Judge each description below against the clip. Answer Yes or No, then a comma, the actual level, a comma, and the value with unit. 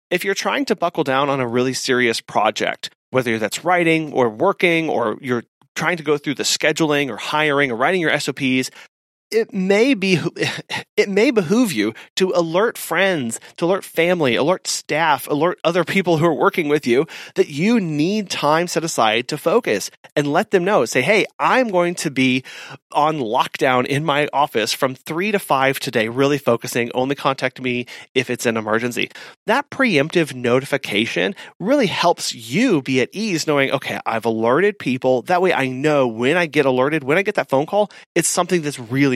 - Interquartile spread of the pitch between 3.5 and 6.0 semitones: Yes, wide, 5.6 semitones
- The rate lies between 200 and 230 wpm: No, average, 185 wpm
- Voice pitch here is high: No, medium, 150 Hz